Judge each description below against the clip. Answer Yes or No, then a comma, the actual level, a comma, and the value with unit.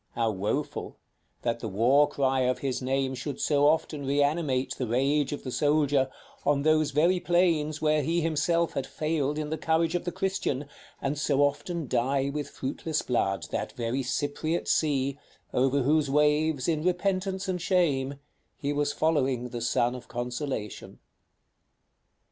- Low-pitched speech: No, medium, 145 Hz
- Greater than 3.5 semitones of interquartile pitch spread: No, average, 3.1 semitones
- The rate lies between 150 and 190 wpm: Yes, average, 155 wpm